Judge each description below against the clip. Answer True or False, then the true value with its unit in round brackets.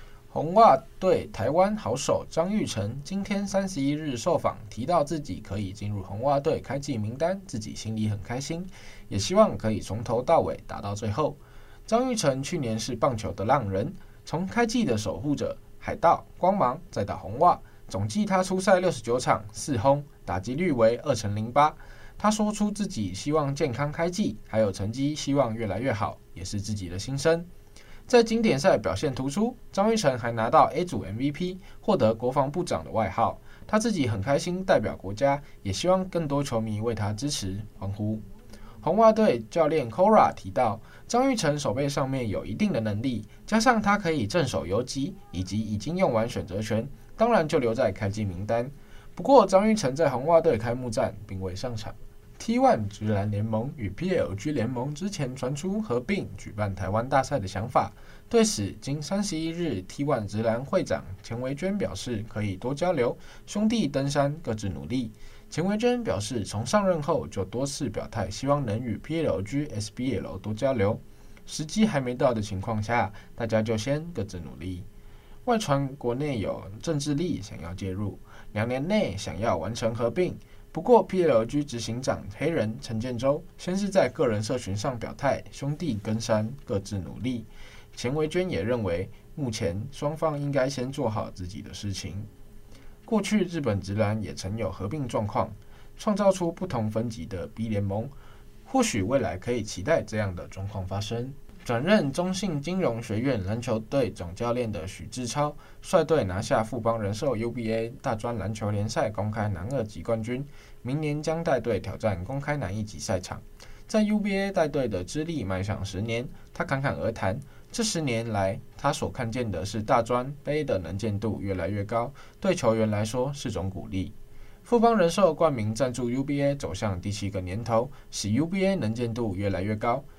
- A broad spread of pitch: True (5.9 semitones)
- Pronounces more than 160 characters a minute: True (270 characters per minute)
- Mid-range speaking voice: False (120 Hz)